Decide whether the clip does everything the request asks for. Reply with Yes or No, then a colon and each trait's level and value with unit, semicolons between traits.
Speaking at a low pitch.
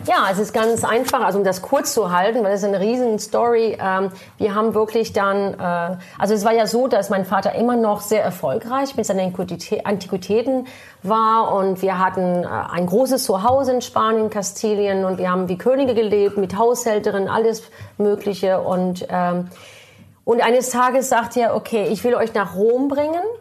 No: high, 215 Hz